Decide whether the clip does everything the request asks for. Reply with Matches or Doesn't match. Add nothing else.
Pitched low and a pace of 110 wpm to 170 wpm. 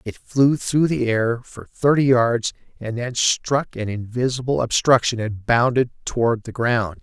Matches